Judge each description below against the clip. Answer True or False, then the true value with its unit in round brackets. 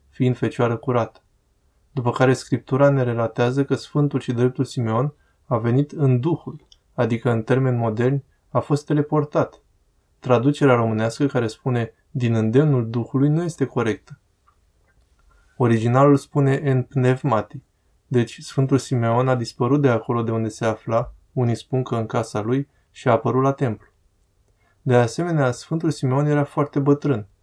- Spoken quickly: False (145 wpm)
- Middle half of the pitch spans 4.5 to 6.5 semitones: False (3.4 semitones)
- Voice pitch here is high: False (125 Hz)